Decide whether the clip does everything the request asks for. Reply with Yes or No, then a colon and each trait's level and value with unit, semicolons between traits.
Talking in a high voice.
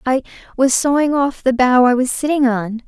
Yes: very high, 260 Hz